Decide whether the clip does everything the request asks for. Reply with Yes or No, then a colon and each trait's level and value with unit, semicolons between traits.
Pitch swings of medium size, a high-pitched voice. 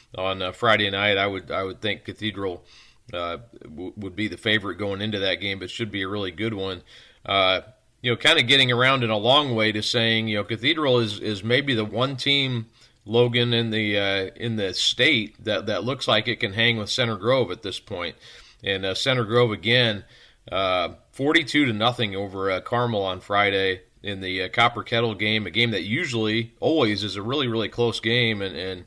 No: average, 3.2 semitones; low, 110 Hz